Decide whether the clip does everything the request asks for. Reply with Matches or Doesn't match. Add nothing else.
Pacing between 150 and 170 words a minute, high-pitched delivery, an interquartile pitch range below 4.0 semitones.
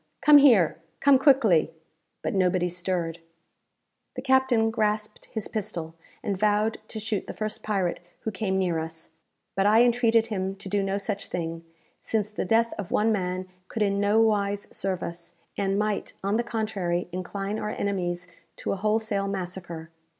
Matches